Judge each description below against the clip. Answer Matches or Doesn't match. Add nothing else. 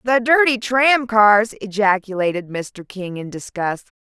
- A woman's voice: Matches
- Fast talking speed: Doesn't match